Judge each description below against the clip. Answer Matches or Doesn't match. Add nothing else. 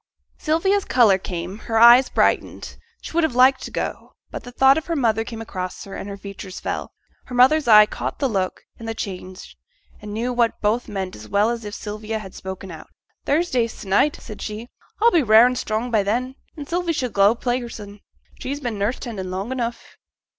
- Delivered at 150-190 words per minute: Doesn't match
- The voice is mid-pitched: Doesn't match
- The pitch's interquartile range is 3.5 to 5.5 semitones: Matches